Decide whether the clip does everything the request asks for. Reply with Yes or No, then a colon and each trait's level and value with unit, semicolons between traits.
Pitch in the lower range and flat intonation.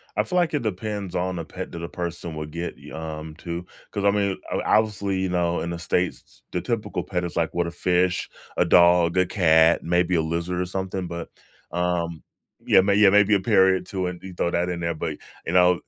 Yes: very low, 90 Hz; narrow, 1.9 semitones